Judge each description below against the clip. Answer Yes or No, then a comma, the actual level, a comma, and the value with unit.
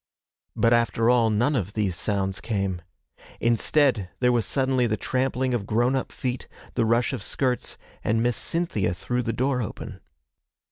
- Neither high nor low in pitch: No, low, 120 Hz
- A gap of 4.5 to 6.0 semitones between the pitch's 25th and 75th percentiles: No, average, 2.9 semitones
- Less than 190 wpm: Yes, average, 160 wpm